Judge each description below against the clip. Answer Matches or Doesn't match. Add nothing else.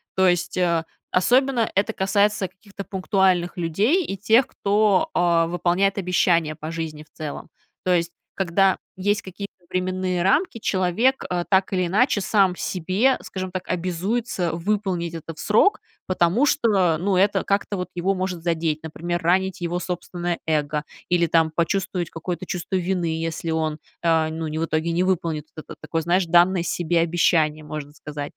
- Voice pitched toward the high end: Doesn't match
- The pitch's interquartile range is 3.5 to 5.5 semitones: Doesn't match